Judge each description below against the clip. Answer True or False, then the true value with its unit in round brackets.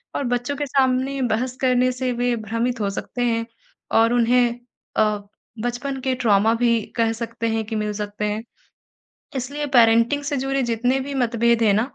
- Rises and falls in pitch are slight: True (2.2 semitones)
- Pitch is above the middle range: True (245 Hz)